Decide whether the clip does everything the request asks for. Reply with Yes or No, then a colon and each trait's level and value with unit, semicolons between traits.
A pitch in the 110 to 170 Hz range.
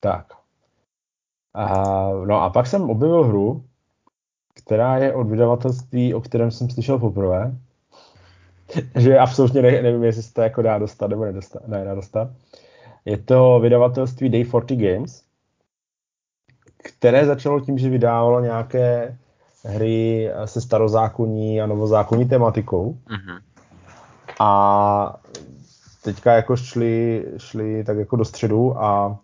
Yes: low, 115 Hz